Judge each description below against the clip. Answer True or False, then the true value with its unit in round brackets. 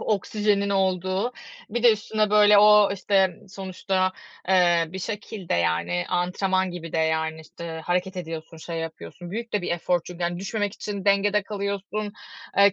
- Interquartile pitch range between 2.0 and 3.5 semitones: True (3.0 semitones)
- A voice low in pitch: False (190 Hz)